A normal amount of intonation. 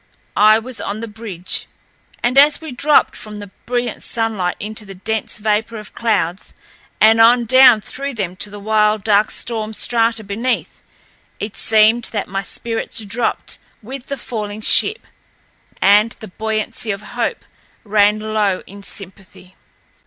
No: narrow, 2.1 semitones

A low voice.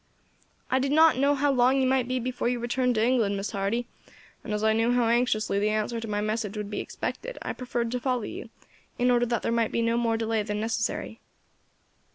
No: high, 235 Hz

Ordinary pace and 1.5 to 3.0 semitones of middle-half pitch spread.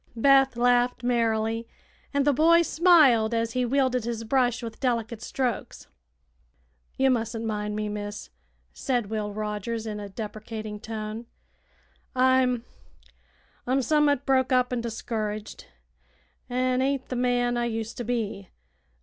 No: slow, 130 wpm; average, 2.7 semitones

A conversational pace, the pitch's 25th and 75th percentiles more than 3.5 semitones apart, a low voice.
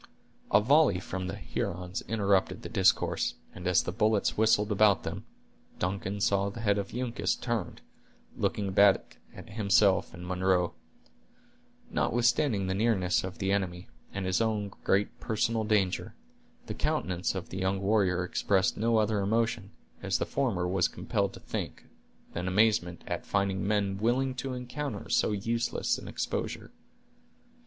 No: average, 150 wpm; average, 2.9 semitones; low, 100 Hz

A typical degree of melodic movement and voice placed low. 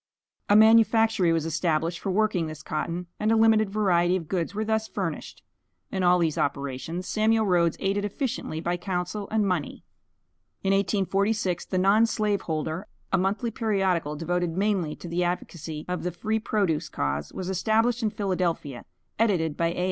No: average, 4.1 semitones; medium, 185 Hz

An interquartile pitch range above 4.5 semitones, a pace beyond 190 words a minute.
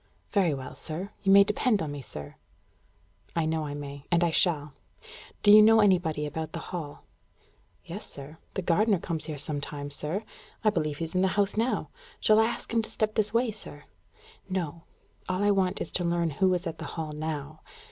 Yes: average, 4.9 semitones; average, 200 wpm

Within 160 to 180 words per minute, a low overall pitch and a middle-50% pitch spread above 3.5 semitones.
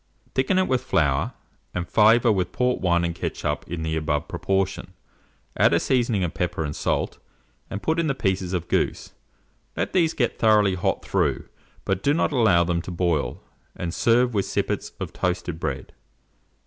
Yes: average, 175 wpm; very low, 95 Hz; wide, 5.6 semitones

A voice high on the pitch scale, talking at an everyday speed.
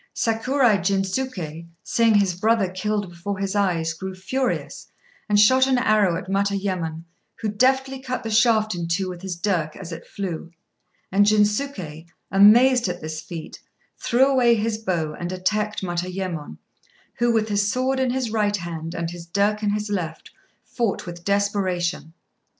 Yes: high, 200 Hz; average, 160 wpm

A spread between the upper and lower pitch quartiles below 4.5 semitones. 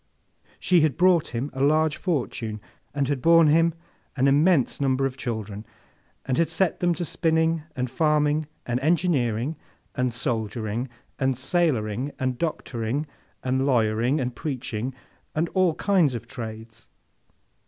No: average, 4.9 semitones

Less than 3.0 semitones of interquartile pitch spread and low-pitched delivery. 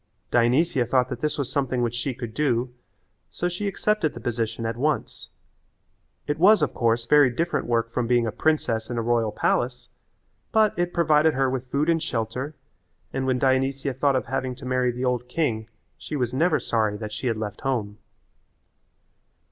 No: average, 4.0 semitones; low, 125 Hz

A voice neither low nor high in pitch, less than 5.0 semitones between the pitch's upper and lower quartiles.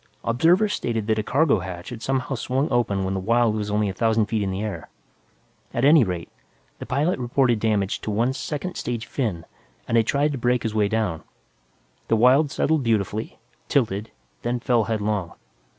No: low, 115 Hz; average, 3.7 semitones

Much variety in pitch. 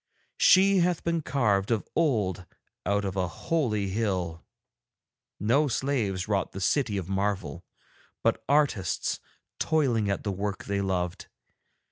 Yes: wide, 6.2 semitones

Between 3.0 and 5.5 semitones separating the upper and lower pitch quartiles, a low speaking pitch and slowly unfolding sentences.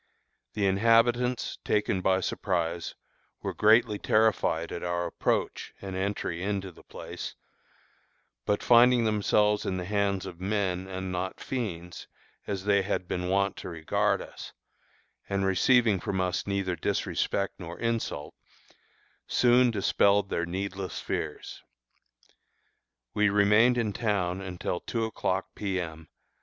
No: narrow, 2.5 semitones; low, 100 Hz; slow, 130 wpm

